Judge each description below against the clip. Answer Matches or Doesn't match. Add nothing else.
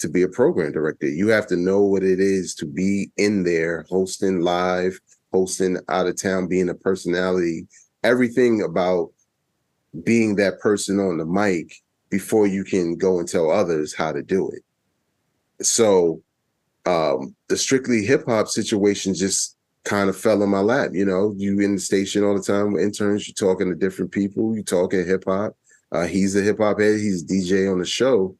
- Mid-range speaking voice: Doesn't match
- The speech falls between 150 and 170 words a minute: Doesn't match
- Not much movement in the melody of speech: Matches